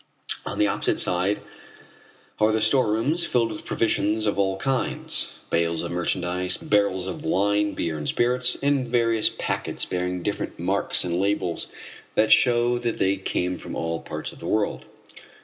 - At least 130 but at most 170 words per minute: Yes, average, 160 wpm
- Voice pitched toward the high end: No, low, 105 Hz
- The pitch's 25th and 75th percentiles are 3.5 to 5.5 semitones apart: Yes, average, 4.2 semitones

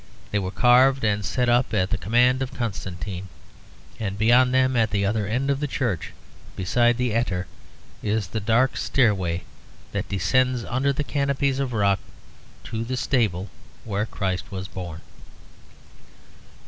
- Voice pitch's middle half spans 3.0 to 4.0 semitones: No, average, 4.5 semitones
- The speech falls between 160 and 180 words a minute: No, average, 150 wpm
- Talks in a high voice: No, low, 115 Hz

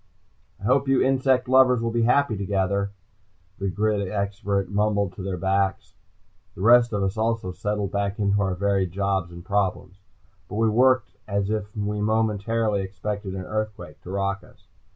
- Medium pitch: No, low, 100 Hz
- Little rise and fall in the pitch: Yes, narrow, 2.2 semitones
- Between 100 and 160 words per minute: No, average, 170 wpm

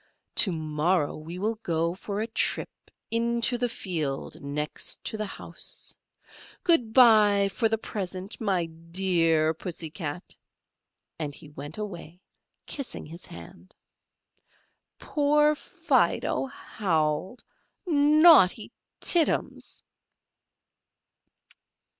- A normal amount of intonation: No, wide, 6.1 semitones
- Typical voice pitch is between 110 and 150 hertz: No, high, 190 Hz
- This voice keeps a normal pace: No, slow, 100 wpm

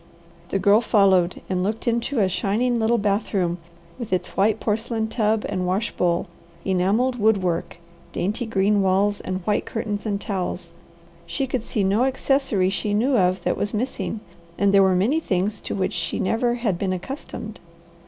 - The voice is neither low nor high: No, high, 205 Hz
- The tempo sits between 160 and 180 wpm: Yes, average, 175 wpm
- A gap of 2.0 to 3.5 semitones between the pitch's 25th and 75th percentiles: Yes, average, 3.2 semitones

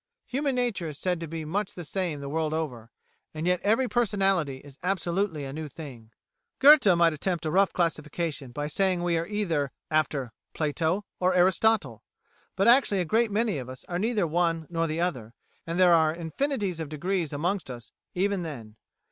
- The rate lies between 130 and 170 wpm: No, average, 180 wpm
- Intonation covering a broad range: No, average, 4.3 semitones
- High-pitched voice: No, medium, 170 Hz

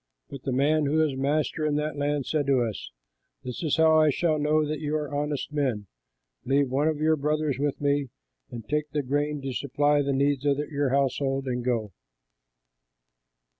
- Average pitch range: No, narrow, 1.9 semitones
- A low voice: No, medium, 145 Hz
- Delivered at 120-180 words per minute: No, average, 190 wpm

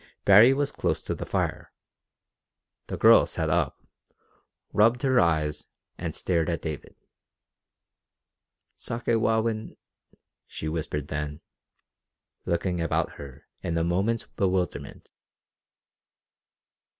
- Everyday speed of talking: No, slow, 100 wpm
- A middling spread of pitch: No, wide, 6.0 semitones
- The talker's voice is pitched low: Yes, very low, 85 Hz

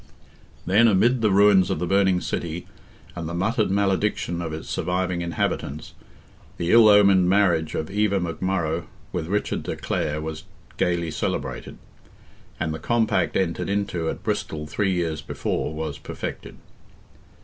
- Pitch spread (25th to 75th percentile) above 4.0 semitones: No, average, 3.6 semitones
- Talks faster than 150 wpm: No, average, 145 wpm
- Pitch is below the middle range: Yes, very low, 90 Hz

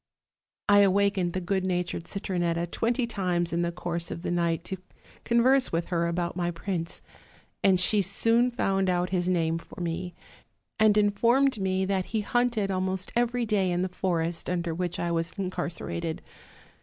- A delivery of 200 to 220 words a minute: No, average, 175 wpm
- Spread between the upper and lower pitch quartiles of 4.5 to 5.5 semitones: No, average, 2.7 semitones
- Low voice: No, medium, 185 Hz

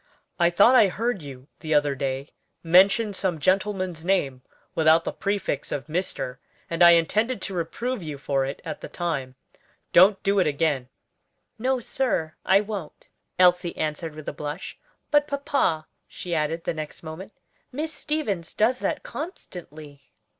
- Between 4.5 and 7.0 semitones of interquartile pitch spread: Yes, average, 5.0 semitones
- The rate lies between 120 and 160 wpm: Yes, average, 155 wpm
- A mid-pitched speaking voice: Yes, medium, 170 Hz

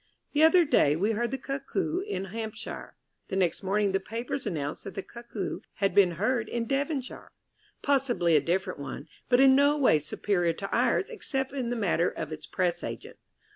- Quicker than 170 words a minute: Yes, average, 185 wpm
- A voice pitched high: Yes, high, 220 Hz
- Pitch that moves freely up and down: Yes, wide, 6.8 semitones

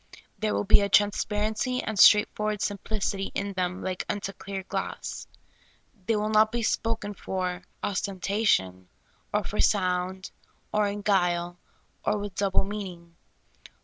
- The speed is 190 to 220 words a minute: No, average, 140 wpm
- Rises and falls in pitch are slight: Yes, narrow, 2.3 semitones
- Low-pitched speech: No, high, 200 Hz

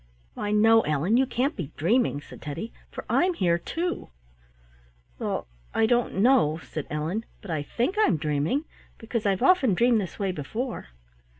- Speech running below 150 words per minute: No, average, 165 wpm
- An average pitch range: No, wide, 7.5 semitones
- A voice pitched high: Yes, high, 210 Hz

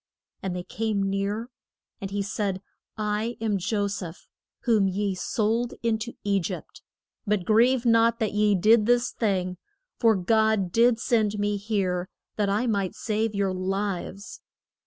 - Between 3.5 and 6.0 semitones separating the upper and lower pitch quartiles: No, narrow, 2.4 semitones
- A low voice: No, high, 210 Hz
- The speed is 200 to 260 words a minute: No, average, 155 wpm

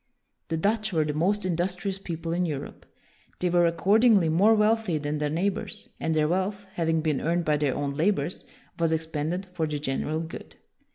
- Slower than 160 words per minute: No, average, 185 wpm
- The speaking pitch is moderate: Yes, medium, 165 Hz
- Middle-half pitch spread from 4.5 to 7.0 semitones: No, average, 3.8 semitones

